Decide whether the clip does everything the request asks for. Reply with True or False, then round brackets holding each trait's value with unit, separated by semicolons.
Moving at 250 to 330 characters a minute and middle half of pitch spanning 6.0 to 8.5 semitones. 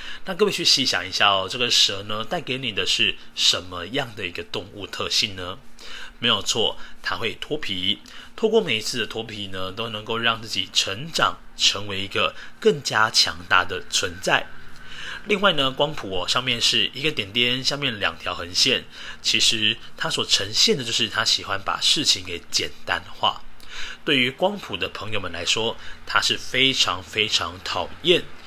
False (255 characters per minute; 5.3 semitones)